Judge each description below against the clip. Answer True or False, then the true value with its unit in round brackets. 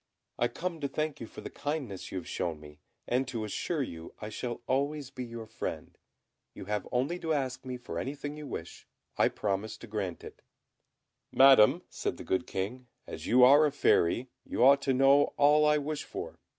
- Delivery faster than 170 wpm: True (200 wpm)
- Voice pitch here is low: True (130 Hz)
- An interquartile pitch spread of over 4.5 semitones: True (5.2 semitones)